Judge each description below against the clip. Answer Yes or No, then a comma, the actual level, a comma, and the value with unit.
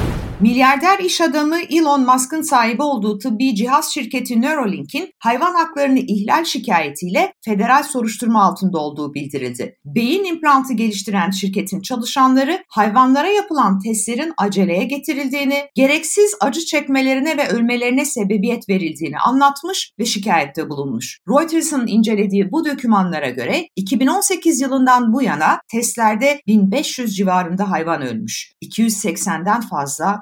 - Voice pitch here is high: Yes, high, 245 Hz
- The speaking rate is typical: Yes, average, 115 wpm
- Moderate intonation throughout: No, wide, 5.9 semitones